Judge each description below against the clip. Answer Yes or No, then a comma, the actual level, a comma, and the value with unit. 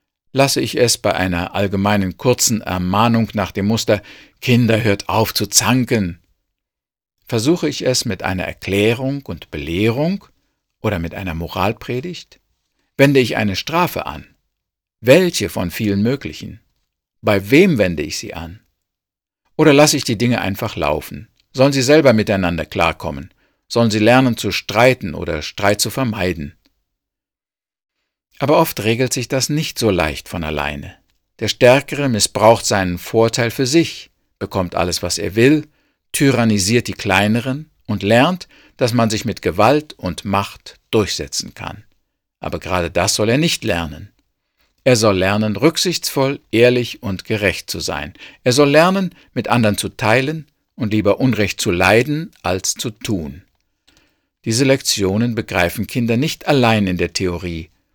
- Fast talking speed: No, average, 145 wpm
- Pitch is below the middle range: Yes, low, 110 Hz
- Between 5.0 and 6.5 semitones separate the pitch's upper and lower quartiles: Yes, wide, 5.4 semitones